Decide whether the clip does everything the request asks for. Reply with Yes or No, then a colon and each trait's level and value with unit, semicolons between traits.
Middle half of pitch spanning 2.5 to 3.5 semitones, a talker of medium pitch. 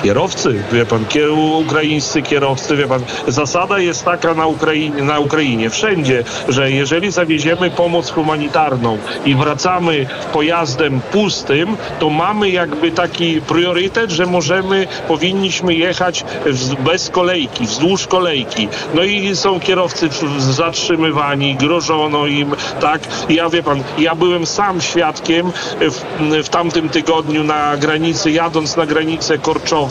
Yes: average, 2.9 semitones; medium, 160 Hz